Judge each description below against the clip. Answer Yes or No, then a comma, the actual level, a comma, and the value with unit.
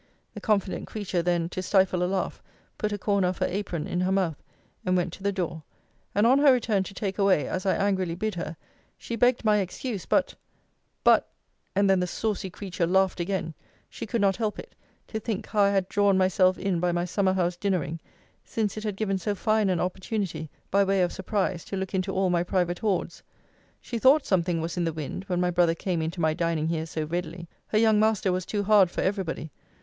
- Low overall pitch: No, high, 190 Hz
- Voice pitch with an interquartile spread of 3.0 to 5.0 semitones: No, narrow, 2.6 semitones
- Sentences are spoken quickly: Yes, fast, 220 wpm